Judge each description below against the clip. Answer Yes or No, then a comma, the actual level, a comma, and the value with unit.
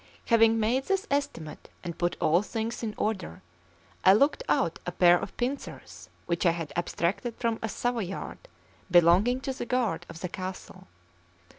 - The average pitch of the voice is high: Yes, high, 210 Hz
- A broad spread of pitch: Yes, wide, 5.7 semitones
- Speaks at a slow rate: No, average, 160 wpm